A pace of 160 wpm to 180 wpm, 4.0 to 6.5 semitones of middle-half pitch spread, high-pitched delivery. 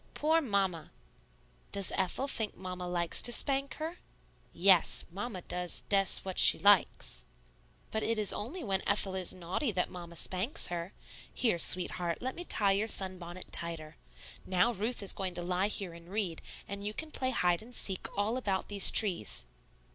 No: average, 170 wpm; average, 3.6 semitones; high, 195 Hz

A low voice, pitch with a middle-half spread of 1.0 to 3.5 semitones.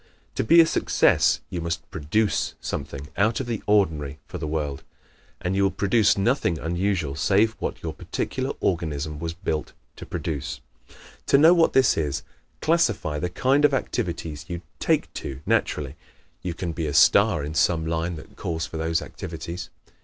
No: very low, 85 Hz; average, 4.8 semitones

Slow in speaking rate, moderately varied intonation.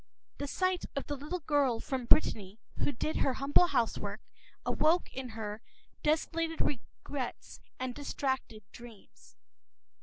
Yes: slow, 125 wpm; average, 4.3 semitones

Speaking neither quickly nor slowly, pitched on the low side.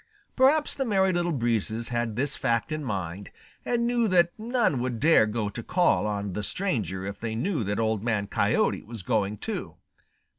Yes: average, 185 wpm; low, 120 Hz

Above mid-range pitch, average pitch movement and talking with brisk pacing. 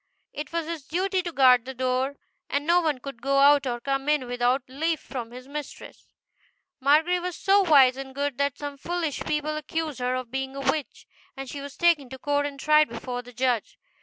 Yes: very high, 280 Hz; average, 3.0 semitones; fast, 215 wpm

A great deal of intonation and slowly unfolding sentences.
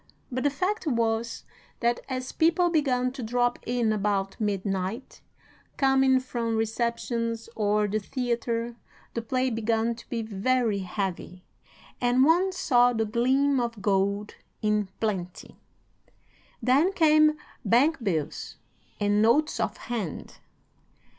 No: average, 3.5 semitones; slow, 120 wpm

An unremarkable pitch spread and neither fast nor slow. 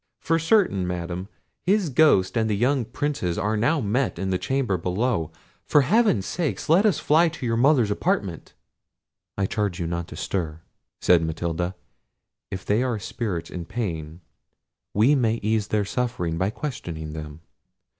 No: wide, 7.2 semitones; average, 155 wpm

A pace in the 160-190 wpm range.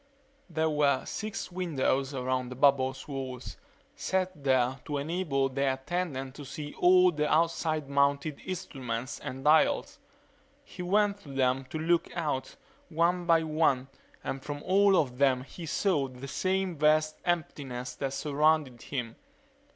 No: average, 145 wpm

